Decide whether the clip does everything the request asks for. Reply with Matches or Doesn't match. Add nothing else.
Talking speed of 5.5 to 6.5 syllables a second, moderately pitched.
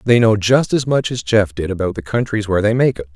Doesn't match